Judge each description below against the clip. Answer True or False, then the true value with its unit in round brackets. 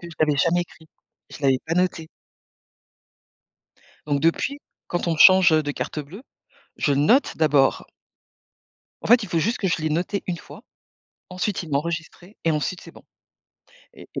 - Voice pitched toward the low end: False (165 Hz)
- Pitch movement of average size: True (3.2 semitones)